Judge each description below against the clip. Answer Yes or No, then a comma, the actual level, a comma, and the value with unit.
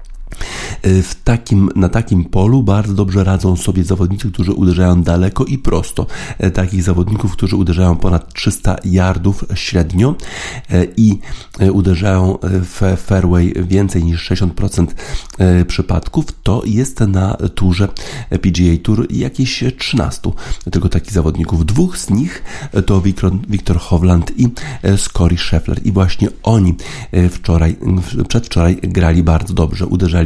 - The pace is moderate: Yes, average, 120 wpm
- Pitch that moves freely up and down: No, narrow, 2.5 semitones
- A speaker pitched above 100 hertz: No, very low, 95 Hz